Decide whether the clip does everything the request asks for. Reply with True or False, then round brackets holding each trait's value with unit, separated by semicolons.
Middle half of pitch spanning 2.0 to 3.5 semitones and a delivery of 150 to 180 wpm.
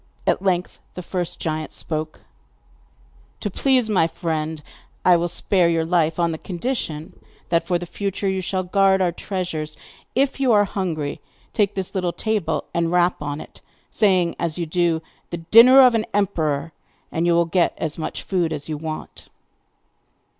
True (3.1 semitones; 170 wpm)